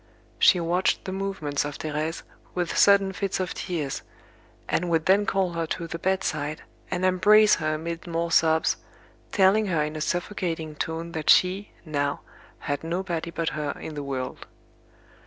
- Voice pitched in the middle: Yes, medium, 165 Hz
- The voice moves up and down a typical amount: Yes, average, 3.3 semitones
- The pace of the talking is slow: No, average, 160 wpm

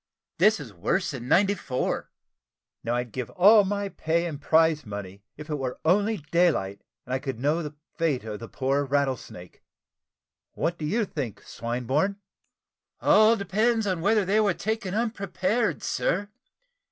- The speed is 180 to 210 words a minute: No, average, 155 wpm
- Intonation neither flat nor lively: No, wide, 7.5 semitones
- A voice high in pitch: No, medium, 165 Hz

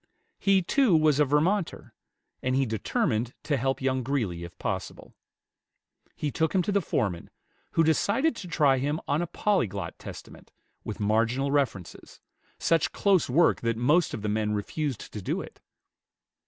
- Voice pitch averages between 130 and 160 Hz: Yes, medium, 140 Hz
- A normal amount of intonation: No, wide, 6.5 semitones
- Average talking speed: Yes, average, 160 wpm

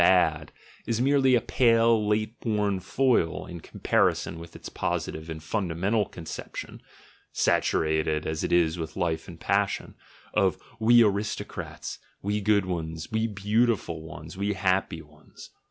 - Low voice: Yes, very low, 95 Hz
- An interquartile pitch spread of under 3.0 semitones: No, average, 5.2 semitones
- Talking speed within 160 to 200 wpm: No, average, 140 wpm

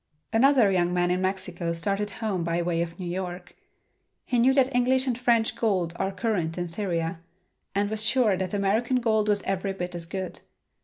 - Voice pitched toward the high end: Yes, high, 195 Hz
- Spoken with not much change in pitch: No, average, 4.1 semitones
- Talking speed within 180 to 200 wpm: Yes, average, 190 wpm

